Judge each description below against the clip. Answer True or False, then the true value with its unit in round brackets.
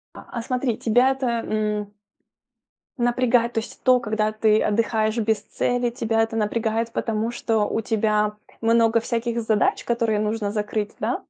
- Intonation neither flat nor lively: False (1.6 semitones)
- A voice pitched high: True (225 Hz)